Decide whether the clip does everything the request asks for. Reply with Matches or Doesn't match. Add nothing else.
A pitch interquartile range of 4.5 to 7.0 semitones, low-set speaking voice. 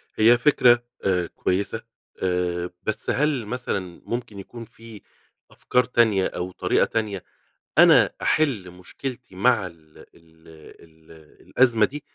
Matches